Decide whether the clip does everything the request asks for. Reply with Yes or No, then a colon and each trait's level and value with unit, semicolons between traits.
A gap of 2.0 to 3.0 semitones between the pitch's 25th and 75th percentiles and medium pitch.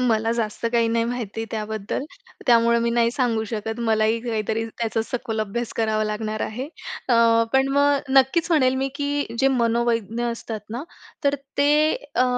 No: average, 2.7 semitones; high, 235 Hz